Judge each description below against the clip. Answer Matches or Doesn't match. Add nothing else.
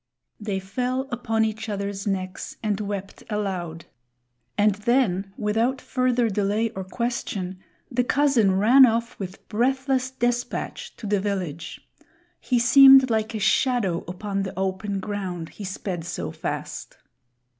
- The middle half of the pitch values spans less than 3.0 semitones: Doesn't match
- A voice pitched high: Matches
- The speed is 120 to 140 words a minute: Matches